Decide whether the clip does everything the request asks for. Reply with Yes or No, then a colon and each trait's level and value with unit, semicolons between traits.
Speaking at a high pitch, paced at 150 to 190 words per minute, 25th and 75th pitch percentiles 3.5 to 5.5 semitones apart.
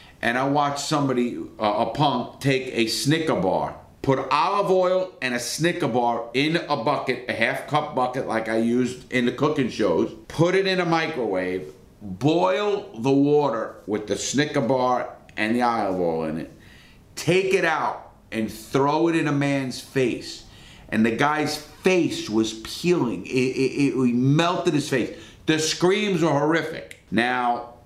No: low, 135 Hz; average, 165 wpm; average, 4.8 semitones